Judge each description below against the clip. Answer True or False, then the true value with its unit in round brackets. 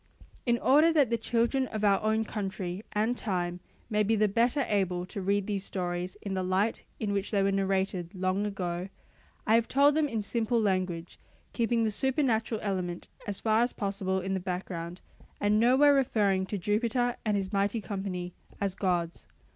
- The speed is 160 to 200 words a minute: True (180 wpm)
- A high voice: True (200 Hz)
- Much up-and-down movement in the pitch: False (3.4 semitones)